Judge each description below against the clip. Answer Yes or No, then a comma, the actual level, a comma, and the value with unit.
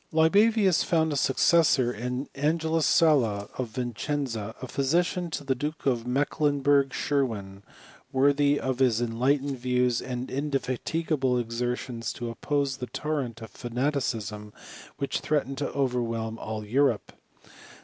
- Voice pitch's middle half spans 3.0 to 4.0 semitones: Yes, average, 3.5 semitones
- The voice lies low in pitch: Yes, low, 130 Hz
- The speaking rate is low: Yes, slow, 125 wpm